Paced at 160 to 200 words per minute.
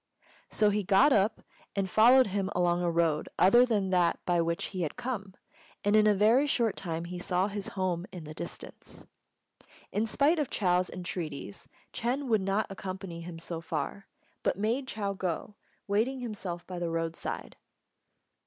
Yes: average, 170 wpm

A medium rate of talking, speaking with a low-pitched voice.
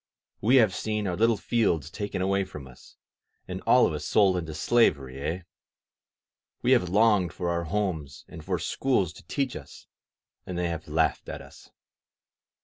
Yes: average, 170 wpm; very low, 90 Hz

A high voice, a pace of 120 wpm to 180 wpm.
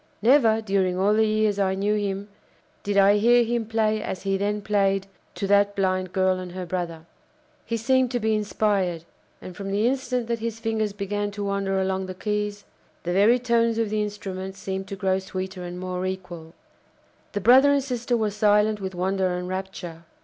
No: high, 200 Hz; average, 195 wpm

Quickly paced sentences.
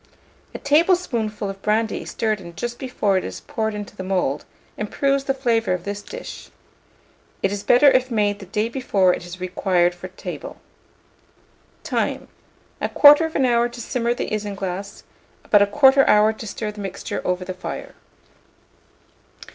No: average, 155 wpm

